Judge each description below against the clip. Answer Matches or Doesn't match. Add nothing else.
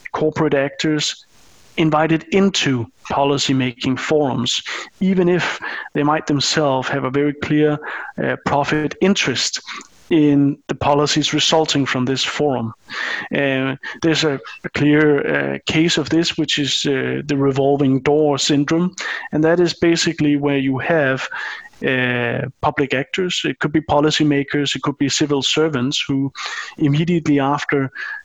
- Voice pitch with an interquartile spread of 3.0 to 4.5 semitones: Doesn't match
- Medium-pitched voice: Matches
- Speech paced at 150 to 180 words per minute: Doesn't match